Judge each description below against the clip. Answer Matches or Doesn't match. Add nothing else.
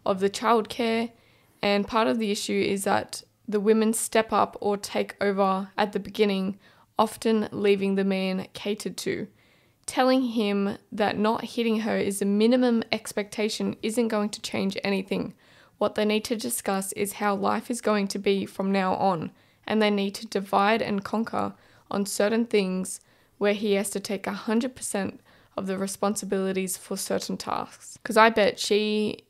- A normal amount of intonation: Doesn't match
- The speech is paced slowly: Doesn't match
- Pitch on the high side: Matches